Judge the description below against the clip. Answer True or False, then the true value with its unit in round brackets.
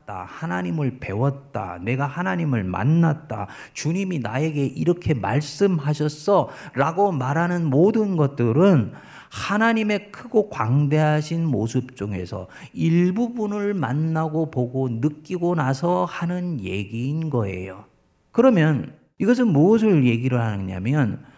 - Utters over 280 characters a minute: False (260 characters per minute)